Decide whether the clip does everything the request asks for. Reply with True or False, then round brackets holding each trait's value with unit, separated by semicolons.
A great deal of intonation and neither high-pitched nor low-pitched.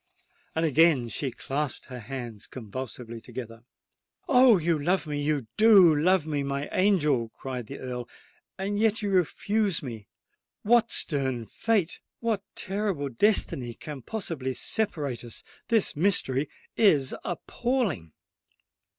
True (7.5 semitones; 150 Hz)